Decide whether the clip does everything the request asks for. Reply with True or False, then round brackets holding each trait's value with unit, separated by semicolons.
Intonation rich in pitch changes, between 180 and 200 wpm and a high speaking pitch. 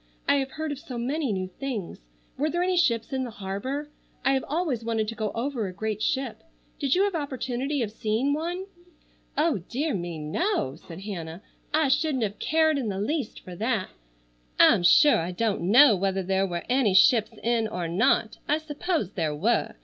True (6.7 semitones; 195 wpm; 240 Hz)